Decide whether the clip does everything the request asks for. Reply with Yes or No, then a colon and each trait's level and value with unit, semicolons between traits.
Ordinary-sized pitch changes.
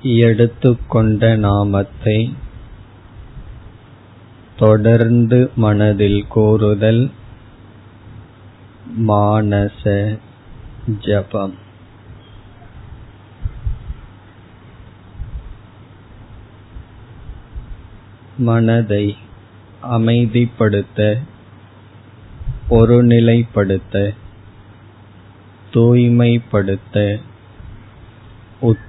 No: narrow, 2.0 semitones